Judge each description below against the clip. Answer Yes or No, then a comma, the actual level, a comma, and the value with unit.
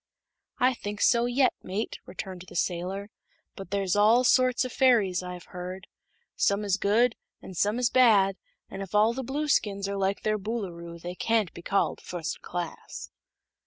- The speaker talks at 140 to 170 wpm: Yes, average, 165 wpm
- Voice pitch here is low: No, high, 200 Hz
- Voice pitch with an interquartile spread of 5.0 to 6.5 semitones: No, average, 4.1 semitones